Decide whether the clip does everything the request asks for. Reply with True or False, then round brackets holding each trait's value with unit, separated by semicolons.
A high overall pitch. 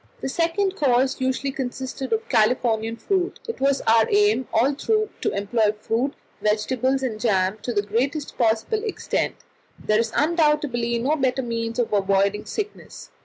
True (255 Hz)